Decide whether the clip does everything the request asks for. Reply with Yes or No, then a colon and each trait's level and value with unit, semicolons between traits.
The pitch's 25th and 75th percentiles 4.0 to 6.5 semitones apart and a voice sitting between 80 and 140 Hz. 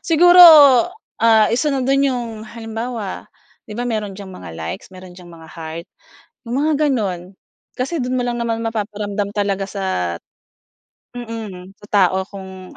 No: average, 4.3 semitones; high, 210 Hz